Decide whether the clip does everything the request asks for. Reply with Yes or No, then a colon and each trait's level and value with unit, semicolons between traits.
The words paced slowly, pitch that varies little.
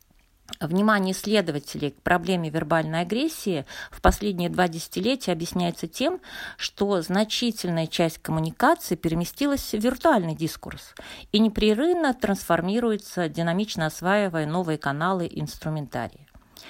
No: slow, 105 wpm; average, 4.7 semitones